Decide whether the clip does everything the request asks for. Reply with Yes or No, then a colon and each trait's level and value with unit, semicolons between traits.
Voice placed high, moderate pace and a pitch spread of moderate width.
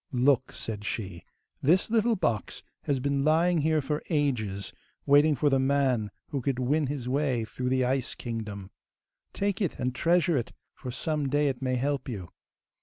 No: low, 135 Hz; average, 175 wpm; average, 3.5 semitones